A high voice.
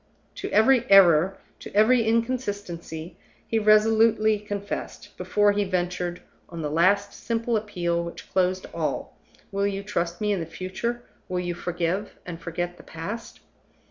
Yes: high, 195 Hz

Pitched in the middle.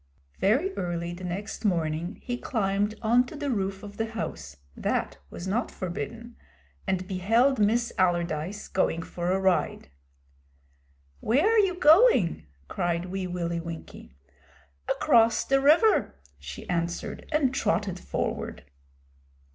No: high, 195 Hz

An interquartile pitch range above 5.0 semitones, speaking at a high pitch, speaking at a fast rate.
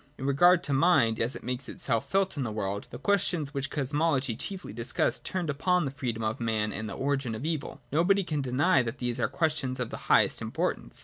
No: wide, 5.4 semitones; medium, 140 Hz; fast, 220 wpm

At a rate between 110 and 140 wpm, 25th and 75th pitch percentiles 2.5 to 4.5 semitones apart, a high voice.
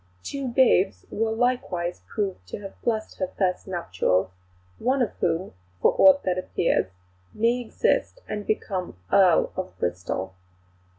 No: slow, 135 wpm; average, 5.3 semitones; high, 195 Hz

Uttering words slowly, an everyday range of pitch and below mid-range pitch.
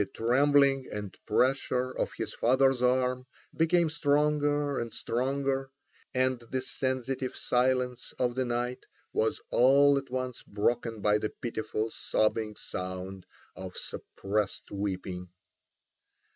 Yes: slow, 115 wpm; average, 3.6 semitones; low, 125 Hz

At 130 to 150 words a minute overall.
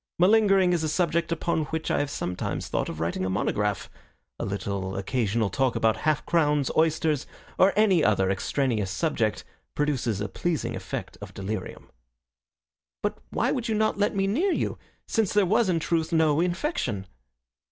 No: average, 165 wpm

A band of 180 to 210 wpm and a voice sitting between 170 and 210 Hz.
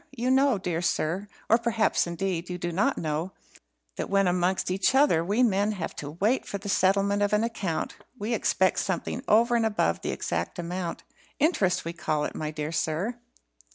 Yes: average, 190 wpm; high, 190 Hz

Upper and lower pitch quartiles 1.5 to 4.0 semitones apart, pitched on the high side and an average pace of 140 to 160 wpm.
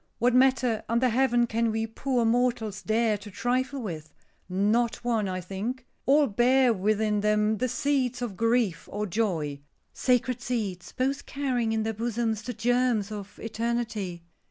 Yes: average, 2.9 semitones; high, 230 Hz; average, 155 wpm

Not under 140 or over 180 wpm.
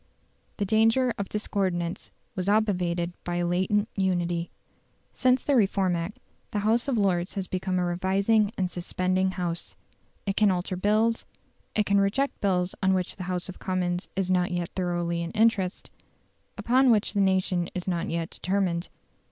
Yes: average, 165 wpm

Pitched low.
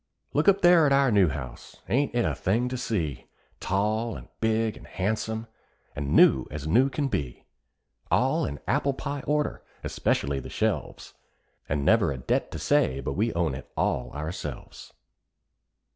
Yes: low, 110 Hz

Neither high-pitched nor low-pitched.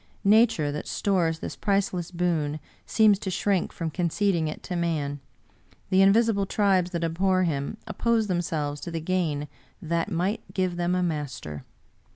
Yes: medium, 175 Hz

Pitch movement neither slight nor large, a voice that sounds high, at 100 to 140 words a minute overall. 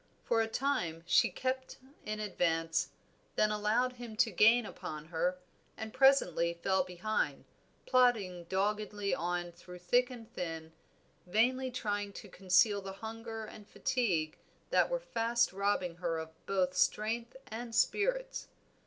Yes: average, 4.9 semitones; high, 210 Hz; slow, 135 wpm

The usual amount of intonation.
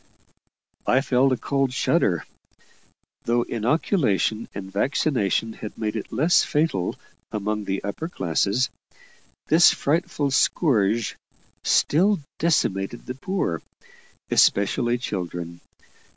No: wide, 6.4 semitones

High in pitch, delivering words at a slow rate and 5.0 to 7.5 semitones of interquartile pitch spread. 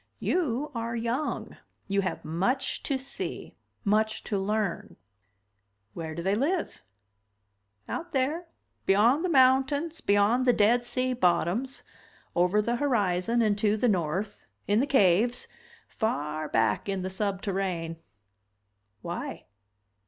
Yes: high, 215 Hz; slow, 125 wpm; average, 5.3 semitones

